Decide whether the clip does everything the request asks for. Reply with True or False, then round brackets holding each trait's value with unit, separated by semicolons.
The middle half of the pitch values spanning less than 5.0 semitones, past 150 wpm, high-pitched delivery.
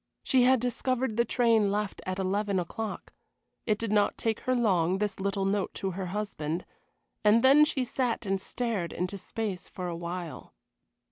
True (3.8 semitones; 175 wpm; 205 Hz)